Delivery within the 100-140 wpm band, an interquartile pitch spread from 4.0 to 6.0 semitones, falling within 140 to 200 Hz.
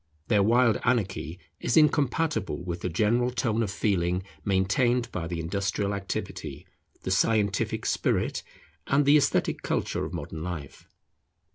No: slow, 135 wpm; average, 5.1 semitones; low, 100 Hz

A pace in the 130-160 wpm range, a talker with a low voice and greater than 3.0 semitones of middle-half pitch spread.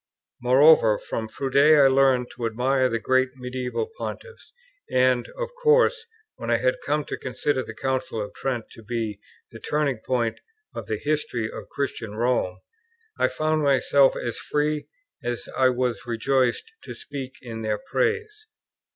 Yes: average, 155 wpm; low, 130 Hz; average, 3.8 semitones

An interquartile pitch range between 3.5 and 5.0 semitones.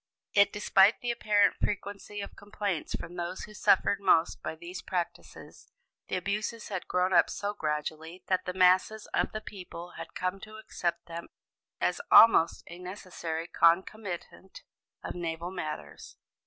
No: average, 3.1 semitones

